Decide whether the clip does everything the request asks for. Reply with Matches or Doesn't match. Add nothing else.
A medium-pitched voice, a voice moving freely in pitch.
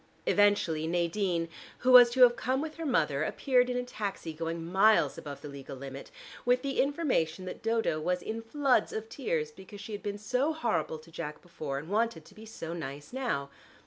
Doesn't match